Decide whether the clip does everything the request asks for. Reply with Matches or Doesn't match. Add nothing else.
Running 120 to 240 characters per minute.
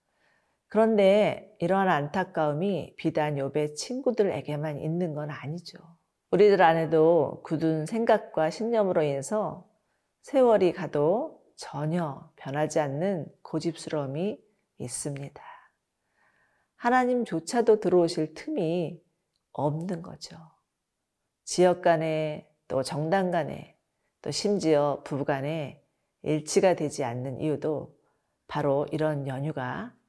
Matches